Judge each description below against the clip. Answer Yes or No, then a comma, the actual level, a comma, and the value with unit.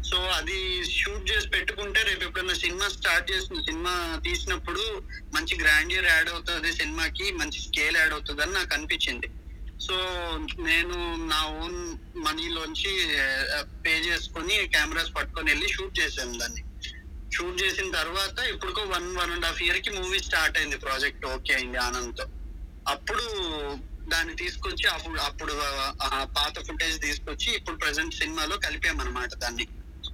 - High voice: No, medium, 175 Hz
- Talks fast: Yes, fast, 130 wpm